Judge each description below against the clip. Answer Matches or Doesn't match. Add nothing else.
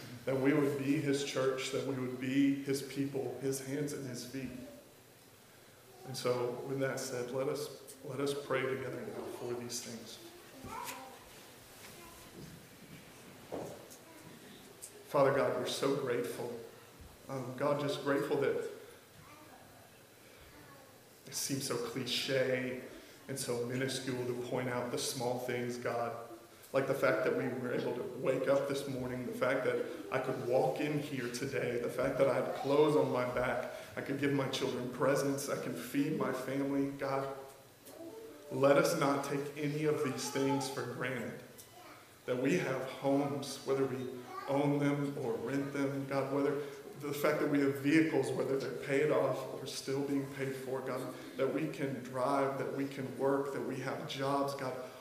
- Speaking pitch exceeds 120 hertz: Matches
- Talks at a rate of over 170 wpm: Doesn't match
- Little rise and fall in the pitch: Matches